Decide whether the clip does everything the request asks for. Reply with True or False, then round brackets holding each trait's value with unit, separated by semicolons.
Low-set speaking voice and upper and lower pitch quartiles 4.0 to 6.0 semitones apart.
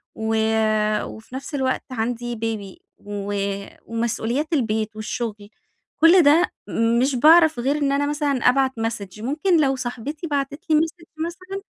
False (265 Hz; 5.2 semitones)